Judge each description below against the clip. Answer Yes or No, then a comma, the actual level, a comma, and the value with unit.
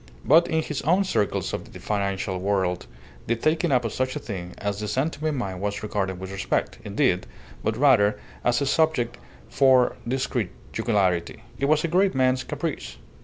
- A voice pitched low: Yes, low, 120 Hz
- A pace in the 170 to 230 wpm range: Yes, average, 180 wpm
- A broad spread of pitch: Yes, wide, 6.2 semitones